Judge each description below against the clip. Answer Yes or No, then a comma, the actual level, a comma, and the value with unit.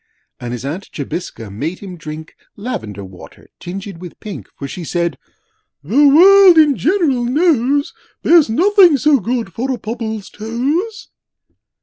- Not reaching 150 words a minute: Yes, average, 140 wpm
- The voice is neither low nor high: No, high, 225 Hz